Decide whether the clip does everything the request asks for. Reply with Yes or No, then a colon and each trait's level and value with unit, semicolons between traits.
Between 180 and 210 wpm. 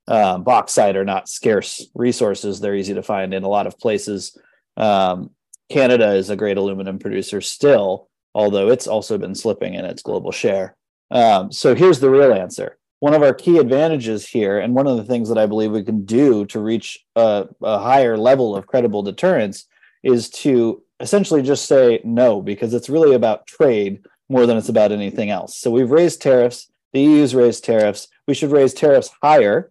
Yes: average, 190 wpm